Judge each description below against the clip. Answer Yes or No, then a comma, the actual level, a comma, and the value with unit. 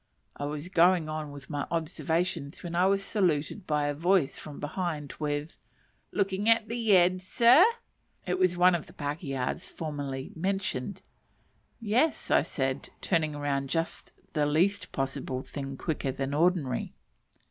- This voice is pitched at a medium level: Yes, medium, 160 Hz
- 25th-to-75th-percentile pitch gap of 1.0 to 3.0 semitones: No, average, 4.4 semitones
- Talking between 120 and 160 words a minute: Yes, average, 145 wpm